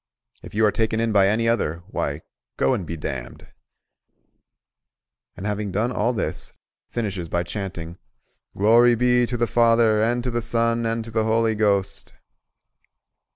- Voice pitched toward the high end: No, low, 110 Hz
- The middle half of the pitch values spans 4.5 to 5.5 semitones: No, average, 3.0 semitones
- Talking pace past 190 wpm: No, average, 155 wpm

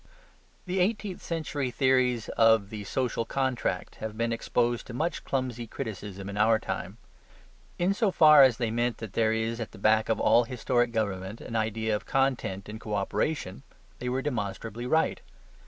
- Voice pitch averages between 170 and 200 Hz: No, low, 115 Hz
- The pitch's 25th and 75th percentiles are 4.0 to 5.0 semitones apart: No, average, 3.2 semitones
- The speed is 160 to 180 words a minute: Yes, average, 170 wpm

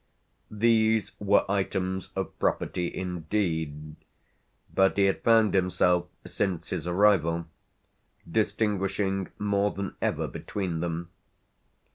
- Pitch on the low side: Yes, very low, 95 Hz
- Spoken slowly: Yes, slow, 100 wpm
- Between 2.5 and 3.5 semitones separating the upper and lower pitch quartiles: Yes, average, 2.8 semitones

